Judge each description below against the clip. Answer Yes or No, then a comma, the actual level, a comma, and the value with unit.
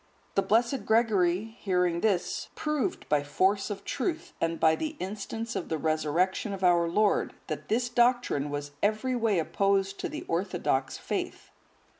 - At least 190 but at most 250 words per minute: No, average, 155 wpm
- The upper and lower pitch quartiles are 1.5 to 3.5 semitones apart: No, average, 5.0 semitones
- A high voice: Yes, high, 195 Hz